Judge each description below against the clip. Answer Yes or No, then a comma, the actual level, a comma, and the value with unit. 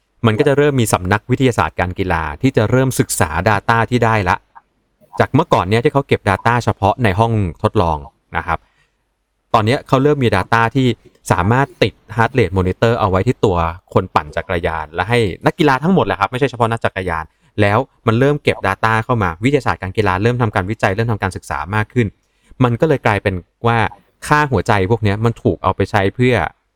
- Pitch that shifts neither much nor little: Yes, average, 4.1 semitones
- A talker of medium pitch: No, low, 110 Hz